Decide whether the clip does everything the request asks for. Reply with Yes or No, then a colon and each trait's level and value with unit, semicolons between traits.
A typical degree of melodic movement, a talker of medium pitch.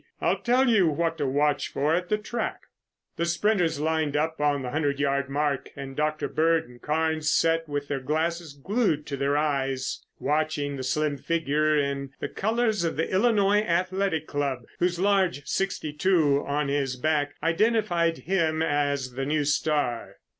Yes: average, 3.1 semitones; medium, 155 Hz